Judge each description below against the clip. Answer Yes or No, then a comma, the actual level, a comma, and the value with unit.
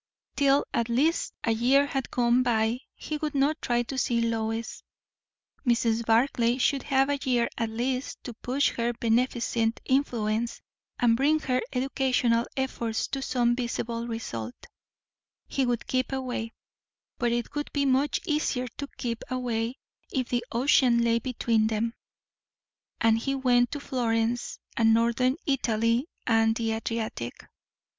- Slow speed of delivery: No, average, 145 wpm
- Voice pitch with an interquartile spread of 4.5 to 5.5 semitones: No, narrow, 2.4 semitones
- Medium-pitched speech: No, high, 240 Hz